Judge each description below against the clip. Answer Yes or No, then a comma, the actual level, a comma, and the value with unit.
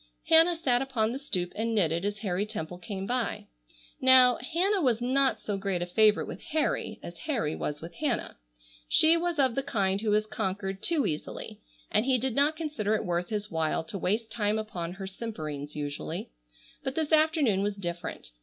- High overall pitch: Yes, high, 215 Hz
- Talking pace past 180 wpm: Yes, average, 190 wpm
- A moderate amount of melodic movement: No, wide, 6.2 semitones